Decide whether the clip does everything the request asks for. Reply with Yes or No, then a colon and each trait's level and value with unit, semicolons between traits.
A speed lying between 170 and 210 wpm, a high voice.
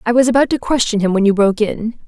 No: fast, 290 wpm; high, 225 Hz